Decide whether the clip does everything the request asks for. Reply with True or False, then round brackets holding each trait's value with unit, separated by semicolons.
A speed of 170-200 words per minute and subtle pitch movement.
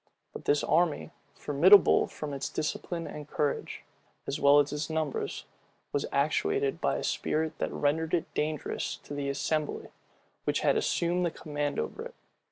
False (160 wpm; 2.1 semitones)